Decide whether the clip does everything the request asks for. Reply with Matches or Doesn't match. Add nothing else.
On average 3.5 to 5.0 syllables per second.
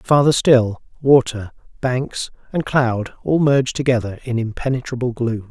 Matches